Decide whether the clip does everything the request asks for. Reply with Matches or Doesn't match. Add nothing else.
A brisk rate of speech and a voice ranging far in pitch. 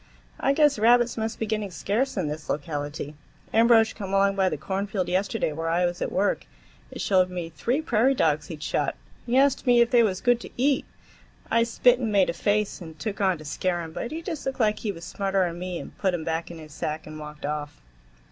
Matches